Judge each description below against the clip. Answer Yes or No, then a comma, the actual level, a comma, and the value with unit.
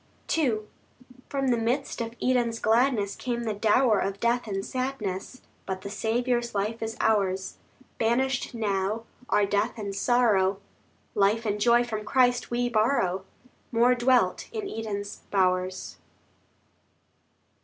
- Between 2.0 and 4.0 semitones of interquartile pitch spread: Yes, average, 3.3 semitones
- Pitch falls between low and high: No, high, 225 Hz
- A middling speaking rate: No, slow, 130 wpm